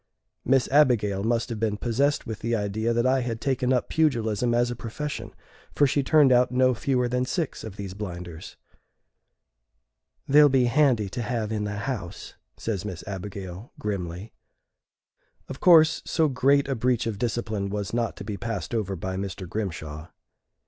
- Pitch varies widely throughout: No, average, 4.0 semitones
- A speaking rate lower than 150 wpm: No, average, 170 wpm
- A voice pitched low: Yes, low, 115 Hz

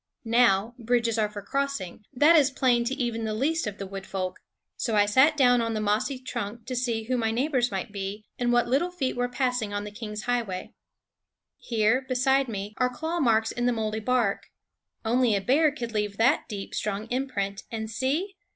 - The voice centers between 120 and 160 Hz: No, high, 235 Hz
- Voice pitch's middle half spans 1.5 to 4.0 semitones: Yes, average, 3.4 semitones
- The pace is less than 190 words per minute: No, average, 200 wpm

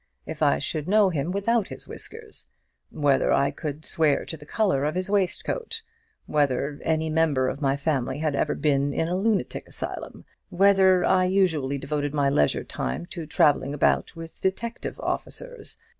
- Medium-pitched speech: Yes, medium, 155 Hz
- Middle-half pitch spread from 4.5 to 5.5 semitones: Yes, average, 5.0 semitones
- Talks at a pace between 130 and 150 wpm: No, average, 165 wpm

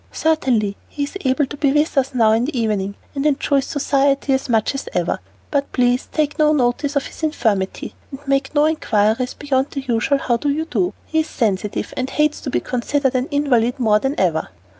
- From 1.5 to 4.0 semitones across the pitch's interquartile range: Yes, average, 3.7 semitones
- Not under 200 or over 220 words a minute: Yes, fast, 205 wpm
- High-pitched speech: Yes, very high, 270 Hz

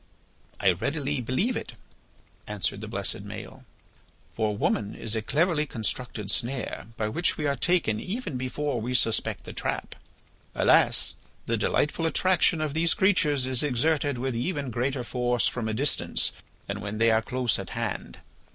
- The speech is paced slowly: No, average, 160 wpm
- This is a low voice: Yes, low, 130 Hz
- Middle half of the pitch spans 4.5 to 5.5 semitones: Yes, average, 5.0 semitones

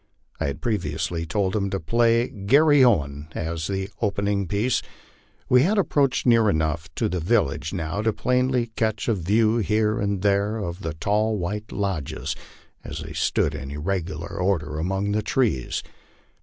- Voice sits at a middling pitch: No, low, 100 Hz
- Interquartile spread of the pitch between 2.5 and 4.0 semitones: No, average, 5.2 semitones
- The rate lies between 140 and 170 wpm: Yes, average, 160 wpm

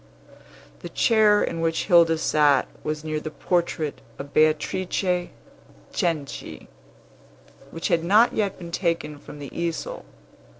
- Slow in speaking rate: Yes, slow, 125 wpm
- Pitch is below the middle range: No, medium, 165 Hz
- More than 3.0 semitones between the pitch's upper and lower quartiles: No, average, 2.7 semitones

